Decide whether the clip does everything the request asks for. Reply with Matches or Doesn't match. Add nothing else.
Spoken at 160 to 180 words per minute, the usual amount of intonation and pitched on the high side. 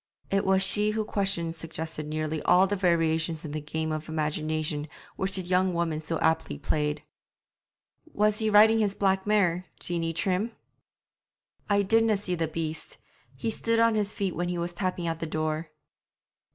Doesn't match